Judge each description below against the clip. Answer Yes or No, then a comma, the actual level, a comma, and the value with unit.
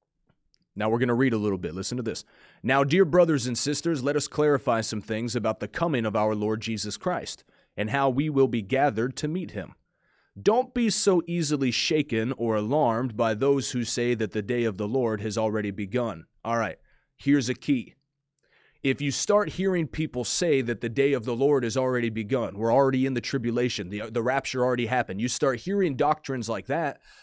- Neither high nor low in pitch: No, low, 125 Hz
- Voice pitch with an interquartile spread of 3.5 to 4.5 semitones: Yes, average, 4.1 semitones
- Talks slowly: No, fast, 205 wpm